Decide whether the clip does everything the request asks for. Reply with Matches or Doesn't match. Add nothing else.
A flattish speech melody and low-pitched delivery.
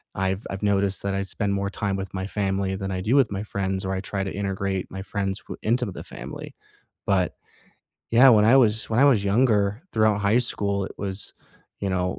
Matches